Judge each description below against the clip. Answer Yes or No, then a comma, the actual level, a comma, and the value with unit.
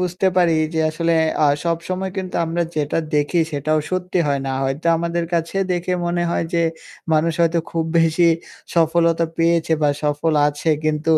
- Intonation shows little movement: Yes, narrow, 1.8 semitones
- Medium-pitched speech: Yes, medium, 165 Hz